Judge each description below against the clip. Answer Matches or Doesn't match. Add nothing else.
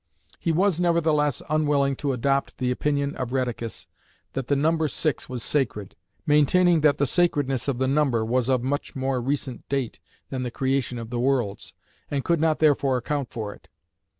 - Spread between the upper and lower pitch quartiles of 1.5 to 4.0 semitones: Matches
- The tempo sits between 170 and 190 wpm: Matches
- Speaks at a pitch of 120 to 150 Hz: Matches